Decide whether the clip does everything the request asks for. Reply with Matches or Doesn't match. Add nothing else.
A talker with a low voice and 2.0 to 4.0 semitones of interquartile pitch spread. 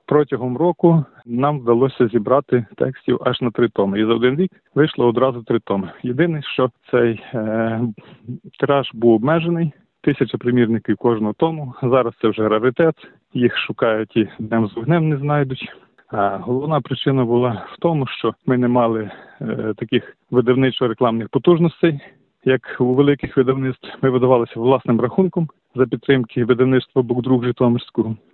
Matches